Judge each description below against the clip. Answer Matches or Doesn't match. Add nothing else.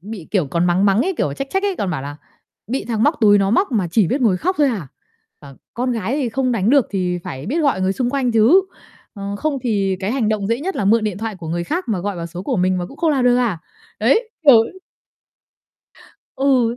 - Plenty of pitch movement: Matches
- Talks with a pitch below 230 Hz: Matches